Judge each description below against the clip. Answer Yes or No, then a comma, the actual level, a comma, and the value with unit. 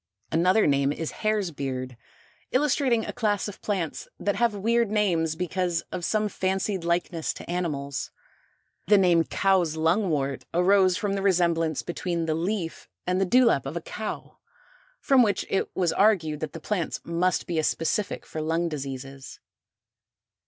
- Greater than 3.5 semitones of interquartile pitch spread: Yes, average, 4.1 semitones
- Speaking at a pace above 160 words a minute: No, average, 155 wpm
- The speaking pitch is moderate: Yes, medium, 175 Hz